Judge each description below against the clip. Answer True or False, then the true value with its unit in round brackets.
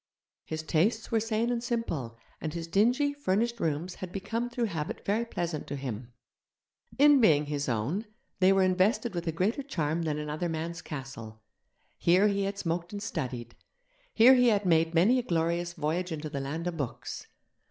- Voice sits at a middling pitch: True (175 Hz)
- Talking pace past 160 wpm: True (180 wpm)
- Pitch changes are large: True (6.2 semitones)